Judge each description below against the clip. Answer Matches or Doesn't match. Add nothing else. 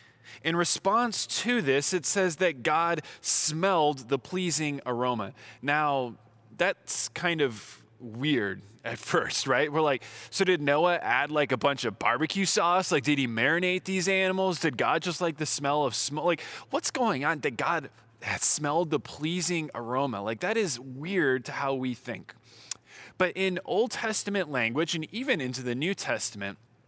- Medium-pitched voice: Matches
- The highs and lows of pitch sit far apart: Matches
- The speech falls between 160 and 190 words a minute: Matches